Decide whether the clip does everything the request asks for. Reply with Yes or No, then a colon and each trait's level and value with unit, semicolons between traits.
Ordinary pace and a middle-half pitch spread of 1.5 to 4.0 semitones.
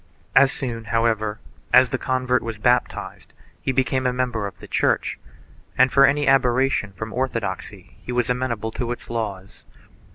Yes: average, 160 wpm; average, 2.7 semitones